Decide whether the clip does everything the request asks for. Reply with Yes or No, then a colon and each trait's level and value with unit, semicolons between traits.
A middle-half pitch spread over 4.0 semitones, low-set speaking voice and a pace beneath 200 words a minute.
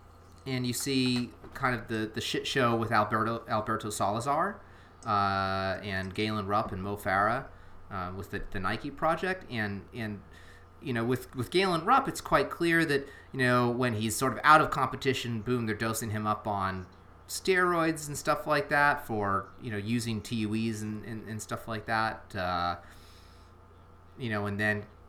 Yes: average, 4.5 semitones; low, 110 Hz; average, 175 wpm